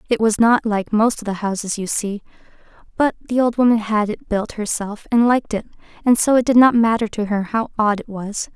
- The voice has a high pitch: Yes, high, 220 Hz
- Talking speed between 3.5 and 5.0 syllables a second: No, 5.5 syllables/s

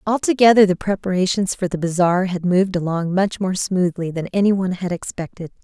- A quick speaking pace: No, average, 180 wpm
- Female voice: Yes, female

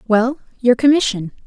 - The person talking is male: No, female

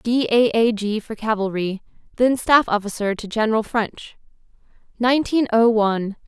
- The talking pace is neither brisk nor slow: Yes, average, 145 wpm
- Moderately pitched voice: No, high, 220 Hz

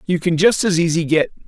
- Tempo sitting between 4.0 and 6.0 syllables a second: Yes, 5.9 syllables/s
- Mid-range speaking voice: Yes, medium, 170 Hz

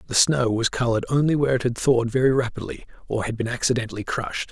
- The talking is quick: Yes, fast, 215 wpm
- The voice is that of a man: Yes, male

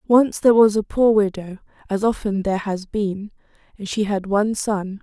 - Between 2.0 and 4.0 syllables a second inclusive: No, 5.1 syllables/s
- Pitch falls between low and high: No, high, 205 Hz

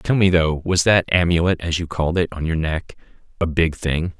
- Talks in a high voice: No, very low, 85 Hz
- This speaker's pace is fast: Yes, fast, 230 wpm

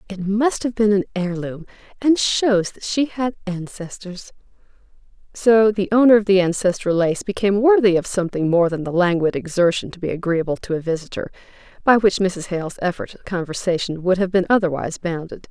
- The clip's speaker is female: Yes, female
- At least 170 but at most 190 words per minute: Yes, average, 180 wpm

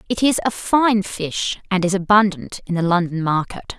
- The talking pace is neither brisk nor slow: Yes, average, 190 wpm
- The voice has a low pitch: No, high, 190 Hz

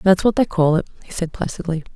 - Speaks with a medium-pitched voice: Yes, medium, 175 Hz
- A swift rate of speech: Yes, fast, 245 wpm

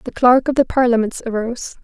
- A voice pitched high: Yes, high, 240 Hz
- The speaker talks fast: No, average, 195 wpm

